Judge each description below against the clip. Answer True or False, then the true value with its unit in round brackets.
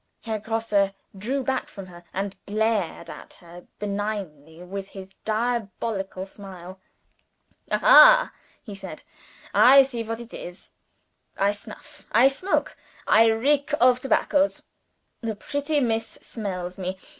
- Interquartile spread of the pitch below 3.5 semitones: False (4.3 semitones)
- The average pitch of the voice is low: False (215 Hz)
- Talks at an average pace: False (125 wpm)